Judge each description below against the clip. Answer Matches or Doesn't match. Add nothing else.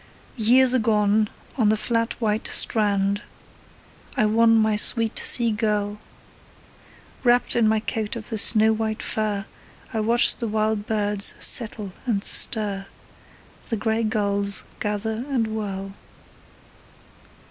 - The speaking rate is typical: Doesn't match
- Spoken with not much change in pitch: Matches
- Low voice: Doesn't match